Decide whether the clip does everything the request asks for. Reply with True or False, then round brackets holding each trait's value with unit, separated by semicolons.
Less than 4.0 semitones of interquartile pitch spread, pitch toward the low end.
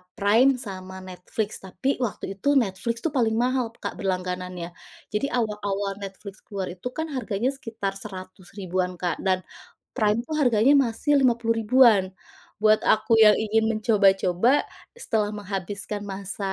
False (3.1 semitones; 210 Hz)